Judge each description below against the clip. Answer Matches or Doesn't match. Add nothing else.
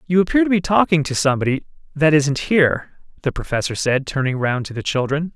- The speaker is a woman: Doesn't match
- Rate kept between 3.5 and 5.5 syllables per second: Doesn't match